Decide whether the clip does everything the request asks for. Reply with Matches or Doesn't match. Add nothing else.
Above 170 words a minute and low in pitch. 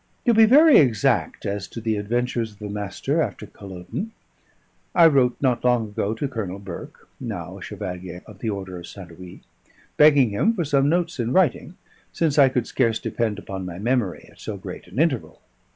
Matches